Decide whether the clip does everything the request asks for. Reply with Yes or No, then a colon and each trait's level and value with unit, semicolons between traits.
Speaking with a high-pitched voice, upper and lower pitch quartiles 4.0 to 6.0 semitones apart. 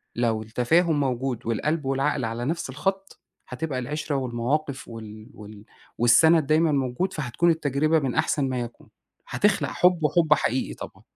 No: low, 135 Hz; average, 4.5 semitones